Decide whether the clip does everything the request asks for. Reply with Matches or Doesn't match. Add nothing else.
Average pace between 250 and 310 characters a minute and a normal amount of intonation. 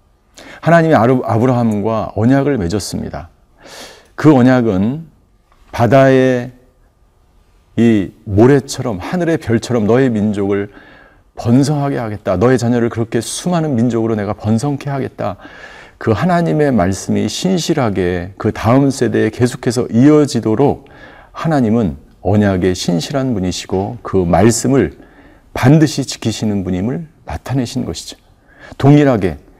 Matches